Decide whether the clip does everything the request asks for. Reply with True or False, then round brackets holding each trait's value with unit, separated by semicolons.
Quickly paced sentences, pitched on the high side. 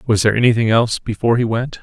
False (230 wpm; 115 Hz)